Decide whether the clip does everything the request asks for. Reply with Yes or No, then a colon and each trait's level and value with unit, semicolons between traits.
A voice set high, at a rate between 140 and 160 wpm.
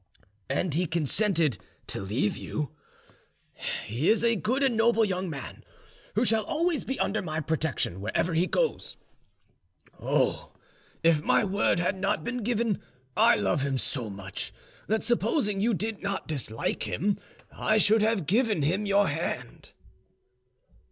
Yes: high, 195 Hz; average, 145 wpm